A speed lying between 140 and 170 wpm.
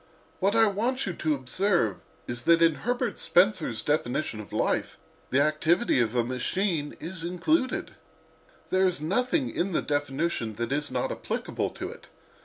Yes: average, 155 wpm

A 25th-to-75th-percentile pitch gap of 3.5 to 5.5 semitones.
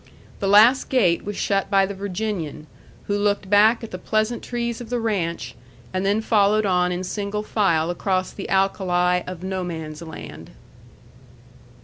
No: average, 3.0 semitones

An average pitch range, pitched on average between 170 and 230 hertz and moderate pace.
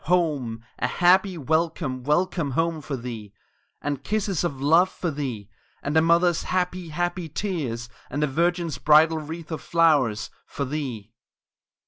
No: average, 4.2 semitones; medium, 155 Hz; average, 145 wpm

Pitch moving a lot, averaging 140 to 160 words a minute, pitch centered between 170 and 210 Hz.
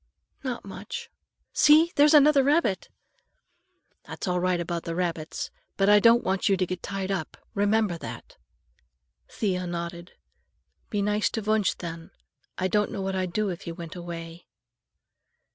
No: average, 3.8 semitones; average, 155 wpm; high, 190 Hz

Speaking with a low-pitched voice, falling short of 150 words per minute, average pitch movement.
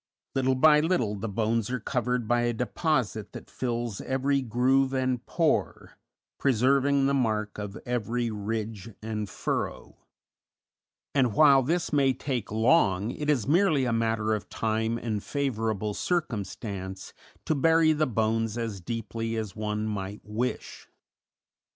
Yes: low, 115 Hz; average, 140 wpm; average, 3.9 semitones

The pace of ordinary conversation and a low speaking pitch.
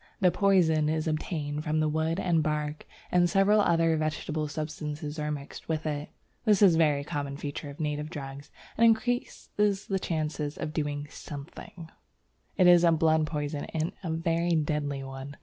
No: average, 170 wpm; medium, 155 Hz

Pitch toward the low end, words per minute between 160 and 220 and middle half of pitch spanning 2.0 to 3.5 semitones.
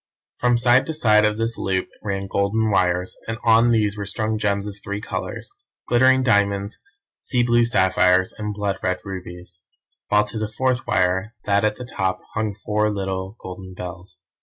Yes: low, 105 Hz; average, 175 wpm; average, 2.9 semitones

